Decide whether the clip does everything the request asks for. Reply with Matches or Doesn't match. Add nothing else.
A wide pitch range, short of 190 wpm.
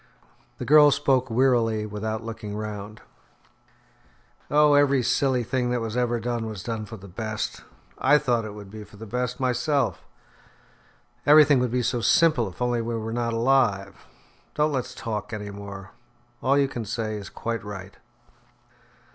Doesn't match